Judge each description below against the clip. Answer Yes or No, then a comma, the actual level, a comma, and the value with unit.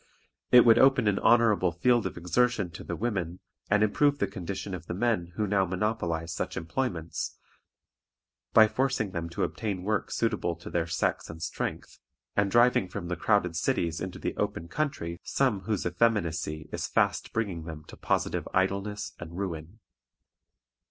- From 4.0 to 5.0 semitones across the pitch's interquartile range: Yes, average, 4.5 semitones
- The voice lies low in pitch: Yes, very low, 95 Hz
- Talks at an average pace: Yes, average, 165 wpm